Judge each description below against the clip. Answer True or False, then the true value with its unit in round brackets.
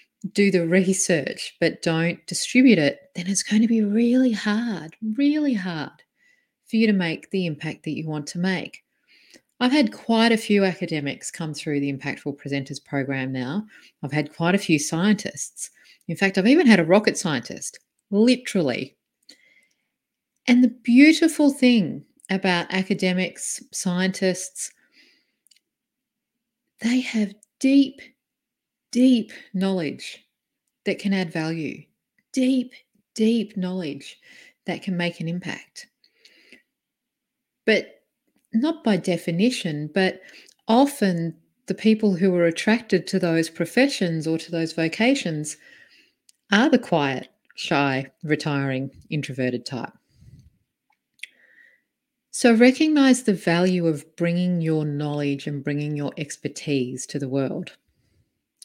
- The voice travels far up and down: True (6.8 semitones)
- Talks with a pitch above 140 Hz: True (190 Hz)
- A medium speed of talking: False (120 wpm)